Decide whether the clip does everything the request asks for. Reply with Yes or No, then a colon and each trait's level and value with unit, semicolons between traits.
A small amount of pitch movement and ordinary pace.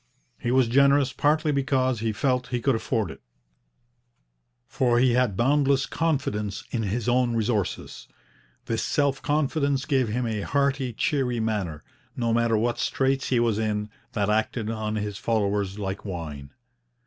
No: average, 3.9 semitones; average, 150 wpm